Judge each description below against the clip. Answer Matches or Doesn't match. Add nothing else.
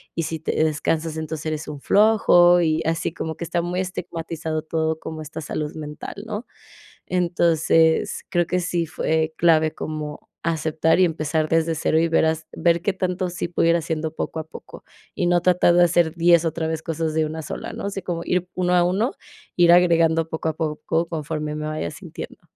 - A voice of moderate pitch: Matches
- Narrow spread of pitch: Matches